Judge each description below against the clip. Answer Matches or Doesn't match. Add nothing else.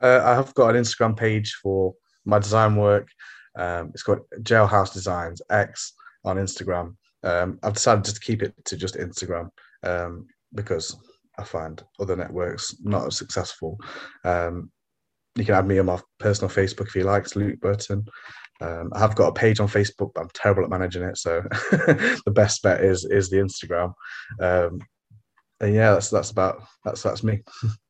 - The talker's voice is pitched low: Matches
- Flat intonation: Doesn't match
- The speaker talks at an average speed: Matches